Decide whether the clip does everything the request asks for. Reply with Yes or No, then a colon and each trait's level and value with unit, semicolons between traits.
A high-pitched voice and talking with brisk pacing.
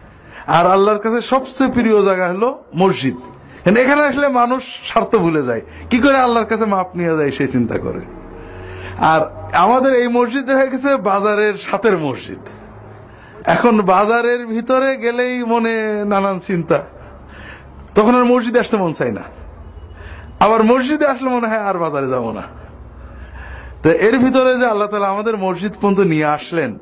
Yes: high, 205 Hz; fast, 140 wpm